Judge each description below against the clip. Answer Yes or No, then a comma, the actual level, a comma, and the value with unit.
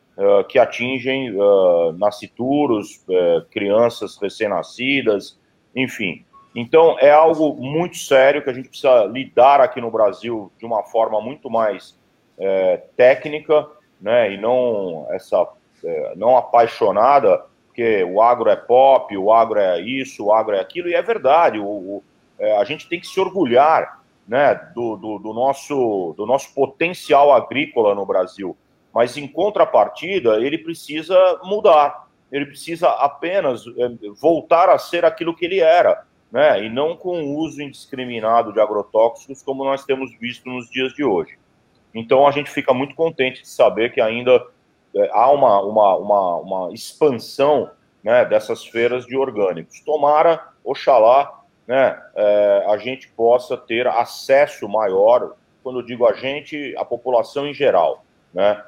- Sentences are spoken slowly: No, average, 150 wpm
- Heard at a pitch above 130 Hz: Yes, medium, 140 Hz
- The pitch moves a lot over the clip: Yes, wide, 6.0 semitones